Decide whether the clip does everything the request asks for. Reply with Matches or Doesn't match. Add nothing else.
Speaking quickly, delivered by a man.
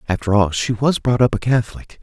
Matches